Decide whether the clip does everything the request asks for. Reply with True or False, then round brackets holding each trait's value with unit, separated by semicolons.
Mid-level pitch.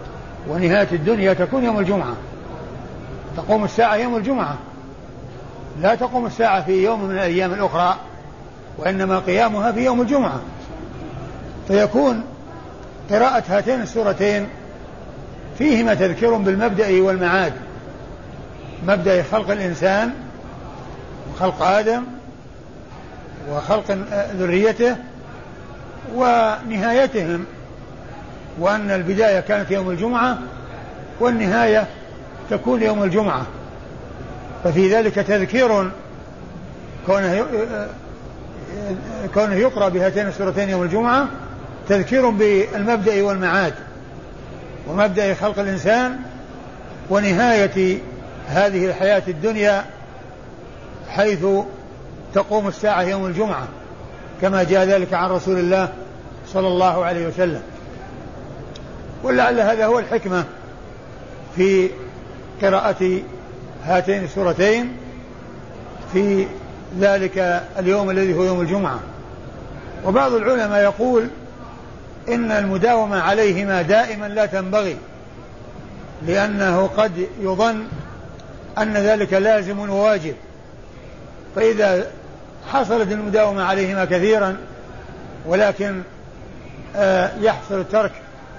False (195 Hz)